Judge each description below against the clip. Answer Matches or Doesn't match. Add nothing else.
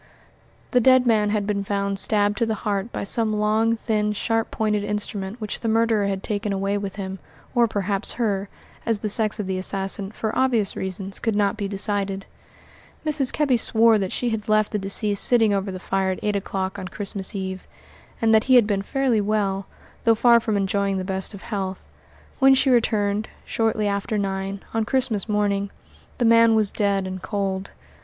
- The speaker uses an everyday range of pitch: Doesn't match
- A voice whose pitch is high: Matches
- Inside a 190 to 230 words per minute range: Matches